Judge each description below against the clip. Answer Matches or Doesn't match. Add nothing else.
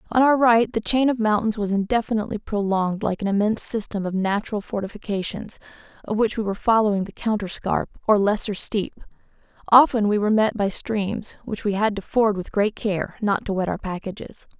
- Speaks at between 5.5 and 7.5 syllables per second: Matches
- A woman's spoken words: Matches